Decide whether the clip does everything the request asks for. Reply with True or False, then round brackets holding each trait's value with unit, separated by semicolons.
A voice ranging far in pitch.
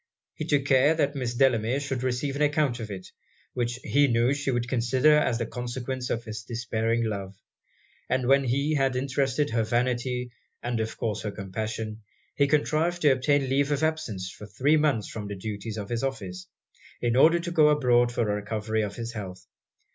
False (3.9 semitones)